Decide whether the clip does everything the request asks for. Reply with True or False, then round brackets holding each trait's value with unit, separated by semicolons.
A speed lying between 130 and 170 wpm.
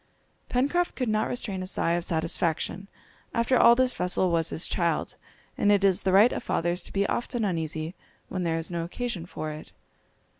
False (190 wpm)